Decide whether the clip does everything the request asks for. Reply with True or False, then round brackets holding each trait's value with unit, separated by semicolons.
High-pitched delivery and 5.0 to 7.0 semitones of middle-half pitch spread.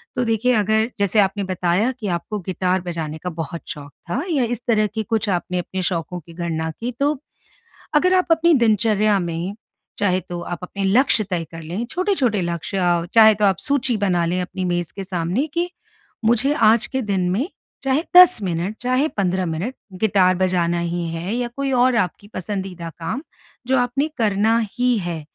True (200 Hz; 5.4 semitones)